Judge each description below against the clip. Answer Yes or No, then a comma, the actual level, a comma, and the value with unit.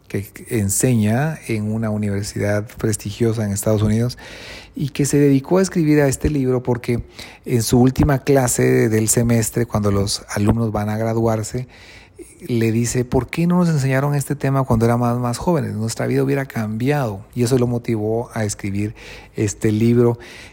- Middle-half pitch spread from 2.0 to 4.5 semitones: Yes, average, 3.4 semitones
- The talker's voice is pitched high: No, low, 120 Hz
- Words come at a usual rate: Yes, average, 165 wpm